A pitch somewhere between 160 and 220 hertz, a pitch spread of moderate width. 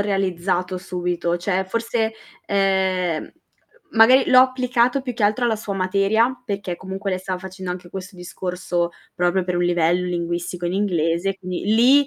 Yes: high, 190 Hz; average, 3.3 semitones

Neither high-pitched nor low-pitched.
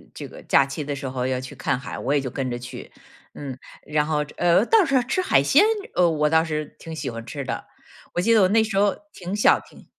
Yes: medium, 150 Hz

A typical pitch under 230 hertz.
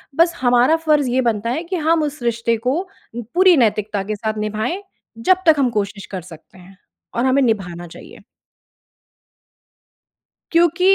No: high, 240 Hz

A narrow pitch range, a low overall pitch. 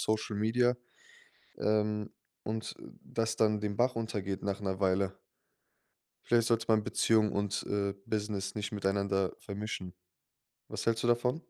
Yes: narrow, 2.1 semitones; low, 105 Hz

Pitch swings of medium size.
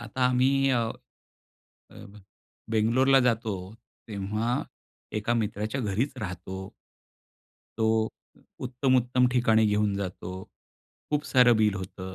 Yes: average, 3.4 semitones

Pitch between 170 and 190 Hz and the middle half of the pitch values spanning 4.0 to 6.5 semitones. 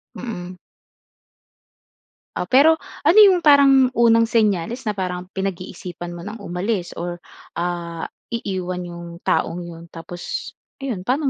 Yes: medium, 185 Hz; average, 4.9 semitones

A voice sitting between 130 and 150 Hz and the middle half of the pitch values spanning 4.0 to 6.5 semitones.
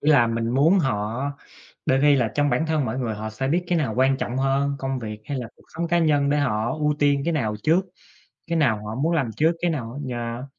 Yes: low, 135 Hz; average, 4.5 semitones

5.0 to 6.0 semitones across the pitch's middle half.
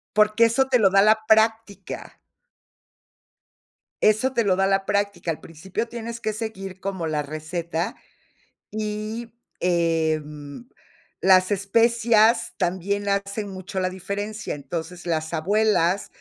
No: average, 3.9 semitones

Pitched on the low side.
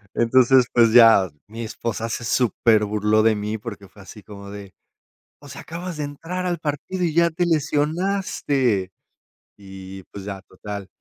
Yes: low, 115 Hz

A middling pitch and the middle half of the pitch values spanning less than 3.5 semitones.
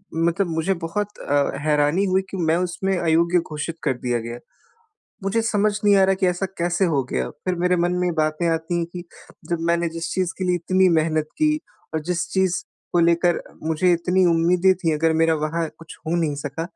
Yes: medium, 170 Hz; narrow, 2.4 semitones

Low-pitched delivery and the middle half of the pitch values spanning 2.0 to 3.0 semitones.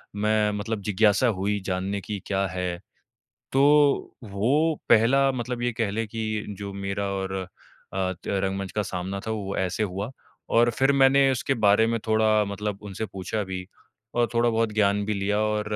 Yes: low, 105 Hz; narrow, 2.5 semitones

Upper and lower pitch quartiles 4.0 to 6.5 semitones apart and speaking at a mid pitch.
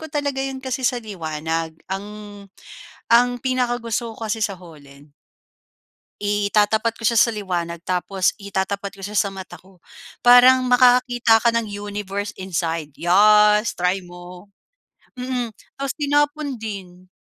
No: average, 4.7 semitones; high, 210 Hz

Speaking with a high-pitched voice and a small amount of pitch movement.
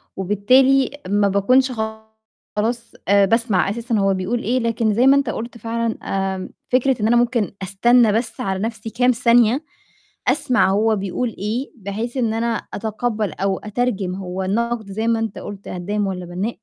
No: high, 220 Hz; average, 3.2 semitones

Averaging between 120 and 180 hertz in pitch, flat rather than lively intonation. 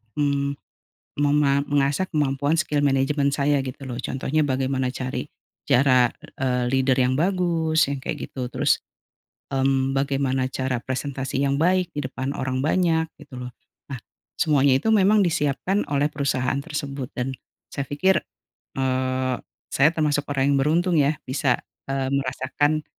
Yes: medium, 140 Hz; narrow, 2.1 semitones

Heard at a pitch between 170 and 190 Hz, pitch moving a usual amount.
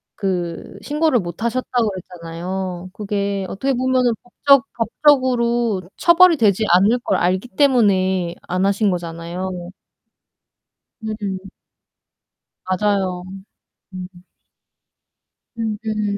No: high, 200 Hz; average, 4.5 semitones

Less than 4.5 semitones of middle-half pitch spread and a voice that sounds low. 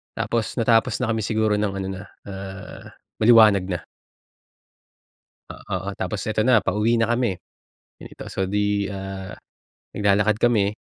Yes: narrow, 2.4 semitones; low, 105 Hz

